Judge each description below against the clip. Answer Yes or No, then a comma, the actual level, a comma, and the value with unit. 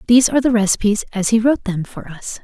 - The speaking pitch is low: No, high, 220 Hz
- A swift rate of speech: Yes, fast, 245 wpm